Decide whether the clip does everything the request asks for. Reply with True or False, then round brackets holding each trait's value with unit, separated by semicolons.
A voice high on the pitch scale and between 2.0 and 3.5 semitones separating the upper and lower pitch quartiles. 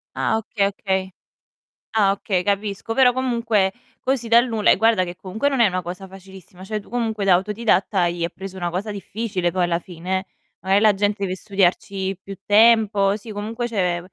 True (200 Hz; 2.8 semitones)